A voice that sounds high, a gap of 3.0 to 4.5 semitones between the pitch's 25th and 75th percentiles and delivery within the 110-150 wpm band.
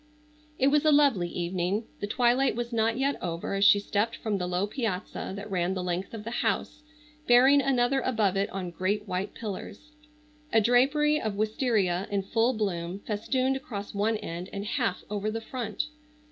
No: high, 215 Hz; average, 4.1 semitones; average, 180 wpm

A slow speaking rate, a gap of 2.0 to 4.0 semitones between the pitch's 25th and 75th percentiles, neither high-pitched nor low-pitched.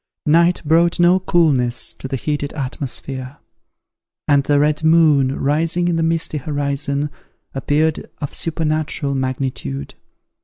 Yes: slow, 120 wpm; average, 2.9 semitones; medium, 150 Hz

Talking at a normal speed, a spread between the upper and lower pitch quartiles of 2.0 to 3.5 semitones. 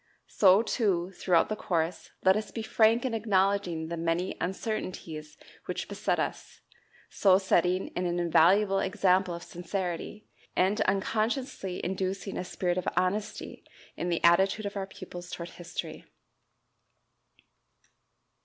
No: slow, 125 wpm; narrow, 2.5 semitones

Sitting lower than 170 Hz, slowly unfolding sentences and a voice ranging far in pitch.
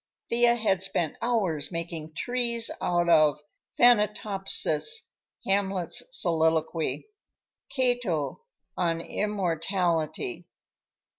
No: high, 190 Hz; slow, 75 wpm; wide, 6.0 semitones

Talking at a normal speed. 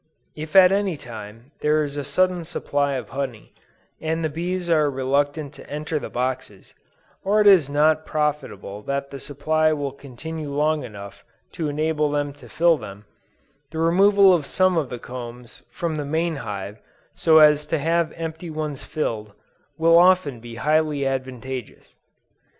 Yes: average, 160 wpm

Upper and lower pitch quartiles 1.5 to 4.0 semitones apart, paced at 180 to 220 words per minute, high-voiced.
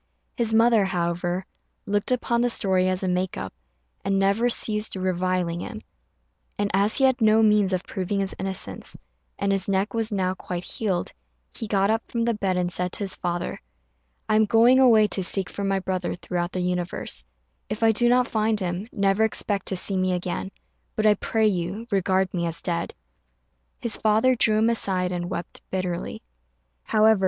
Yes: average, 3.1 semitones; average, 185 wpm; high, 195 Hz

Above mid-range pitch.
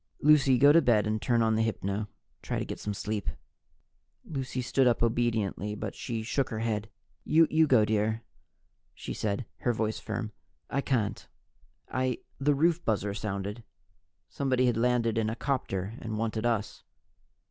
No: low, 115 Hz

